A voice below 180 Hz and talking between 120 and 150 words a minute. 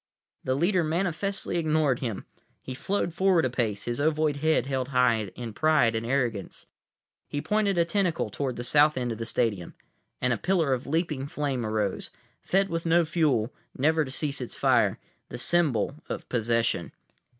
No: medium, 140 Hz; average, 170 wpm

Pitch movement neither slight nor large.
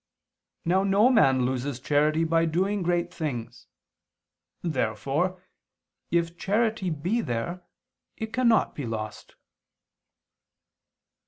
No: wide, 6.1 semitones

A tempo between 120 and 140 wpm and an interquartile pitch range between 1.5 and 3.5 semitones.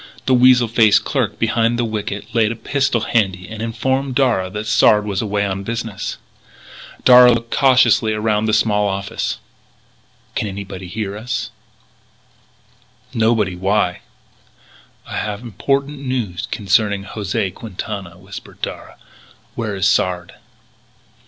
Yes: slow, 135 wpm; average, 2.9 semitones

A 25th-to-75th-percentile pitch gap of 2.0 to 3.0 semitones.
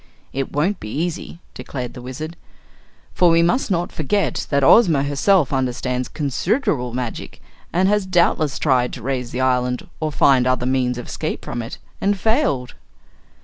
No: wide, 5.6 semitones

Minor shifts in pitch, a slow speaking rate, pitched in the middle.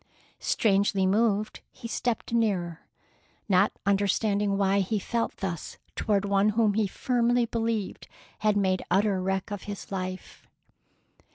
No: narrow, 2.3 semitones; slow, 125 wpm; high, 200 Hz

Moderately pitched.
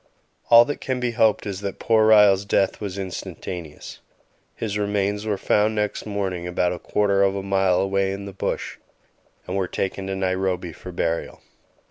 No: low, 100 Hz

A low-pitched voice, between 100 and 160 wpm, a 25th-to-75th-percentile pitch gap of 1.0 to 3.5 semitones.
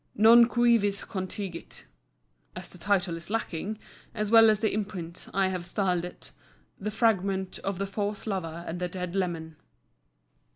No: high, 195 Hz; average, 155 wpm; average, 3.0 semitones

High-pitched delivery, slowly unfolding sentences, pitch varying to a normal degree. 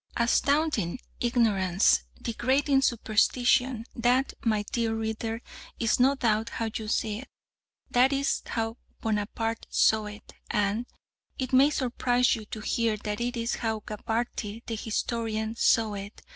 No: high, 230 Hz; slow, 130 wpm; narrow, 2.3 semitones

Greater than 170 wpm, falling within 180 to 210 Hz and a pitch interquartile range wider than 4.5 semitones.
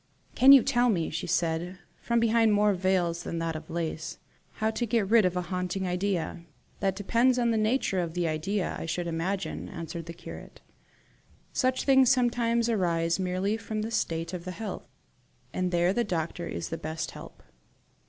Yes: average, 185 wpm; medium, 185 Hz; average, 4.9 semitones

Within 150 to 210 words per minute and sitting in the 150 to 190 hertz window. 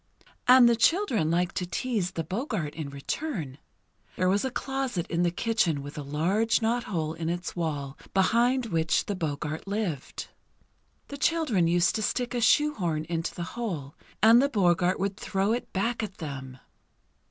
Yes: average, 170 wpm; medium, 185 Hz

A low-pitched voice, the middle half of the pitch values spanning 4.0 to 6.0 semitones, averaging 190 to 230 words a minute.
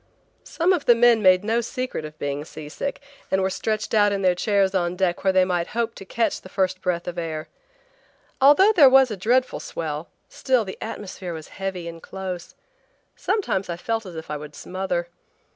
No: high, 190 Hz; average, 4.8 semitones; average, 195 wpm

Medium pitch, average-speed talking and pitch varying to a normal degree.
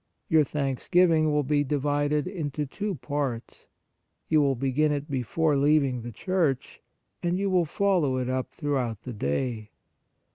Yes: medium, 145 Hz; average, 145 wpm; average, 3.2 semitones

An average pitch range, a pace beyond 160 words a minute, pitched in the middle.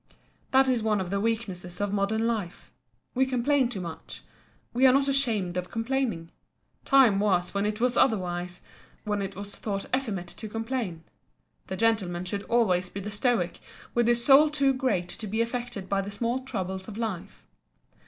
No: average, 4.3 semitones; average, 175 wpm; high, 215 Hz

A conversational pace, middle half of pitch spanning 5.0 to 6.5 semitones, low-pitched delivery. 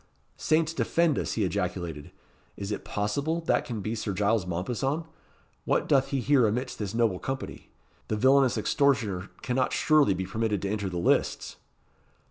Yes: average, 160 wpm; wide, 5.5 semitones; low, 110 Hz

